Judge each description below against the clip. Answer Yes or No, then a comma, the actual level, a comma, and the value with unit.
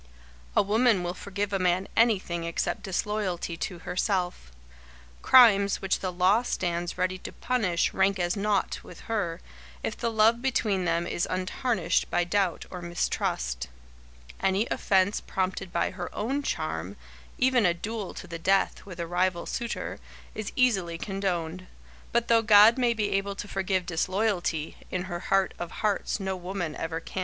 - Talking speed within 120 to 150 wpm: No, average, 160 wpm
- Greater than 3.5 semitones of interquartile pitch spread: No, average, 3.2 semitones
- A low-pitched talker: No, high, 190 Hz